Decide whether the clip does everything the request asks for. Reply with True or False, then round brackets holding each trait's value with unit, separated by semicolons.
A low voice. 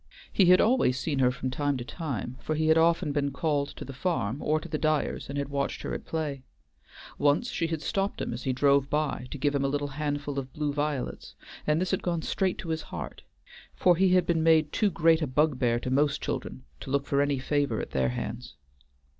False (145 Hz)